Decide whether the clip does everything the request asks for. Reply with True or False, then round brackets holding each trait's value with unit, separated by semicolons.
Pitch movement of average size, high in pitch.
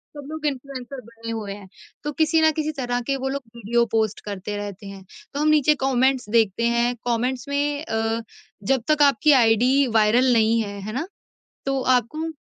True (4.1 semitones; 245 Hz)